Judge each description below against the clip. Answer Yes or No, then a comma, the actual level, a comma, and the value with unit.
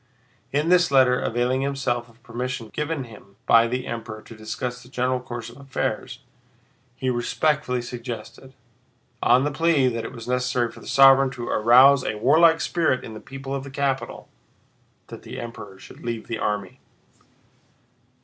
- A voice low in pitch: Yes, low, 125 Hz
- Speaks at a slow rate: No, average, 160 wpm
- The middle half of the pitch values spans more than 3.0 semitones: No, narrow, 2.6 semitones